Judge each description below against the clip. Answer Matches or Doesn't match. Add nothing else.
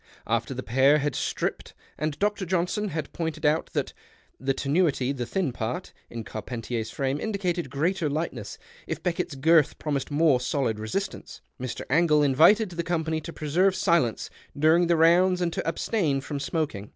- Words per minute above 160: Matches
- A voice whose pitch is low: Doesn't match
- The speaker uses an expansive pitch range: Doesn't match